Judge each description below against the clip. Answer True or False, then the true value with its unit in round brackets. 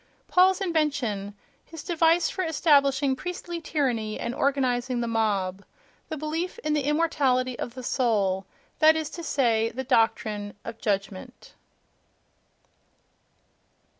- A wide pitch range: True (5.8 semitones)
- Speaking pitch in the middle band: False (265 Hz)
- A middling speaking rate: False (115 wpm)